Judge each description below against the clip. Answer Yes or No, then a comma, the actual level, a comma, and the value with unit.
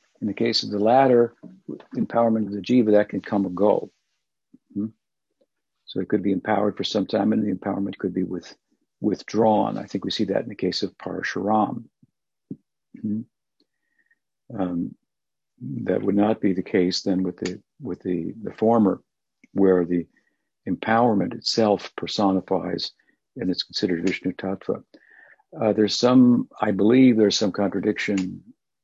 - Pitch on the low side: Yes, low, 100 Hz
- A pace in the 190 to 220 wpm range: No, average, 155 wpm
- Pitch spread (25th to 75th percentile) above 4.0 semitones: No, average, 2.9 semitones